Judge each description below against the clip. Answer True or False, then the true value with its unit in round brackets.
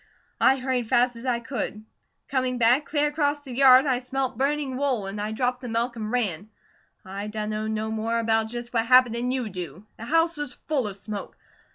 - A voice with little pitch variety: False (3.3 semitones)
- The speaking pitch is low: False (245 Hz)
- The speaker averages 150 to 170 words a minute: False (205 wpm)